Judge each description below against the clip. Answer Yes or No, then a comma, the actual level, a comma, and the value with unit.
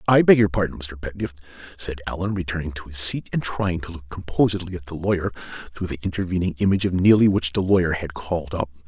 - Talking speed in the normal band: No, fast, 215 wpm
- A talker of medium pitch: No, very low, 85 Hz